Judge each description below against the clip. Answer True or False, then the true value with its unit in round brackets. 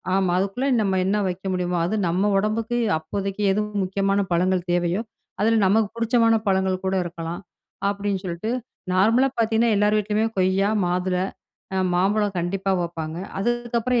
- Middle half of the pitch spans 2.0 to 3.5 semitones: True (2.9 semitones)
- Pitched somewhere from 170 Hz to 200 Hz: True (195 Hz)